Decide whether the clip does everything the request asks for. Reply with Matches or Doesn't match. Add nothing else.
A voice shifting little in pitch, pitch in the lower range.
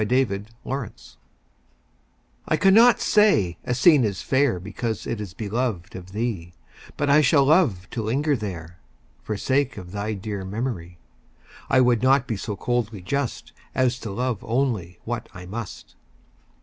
Doesn't match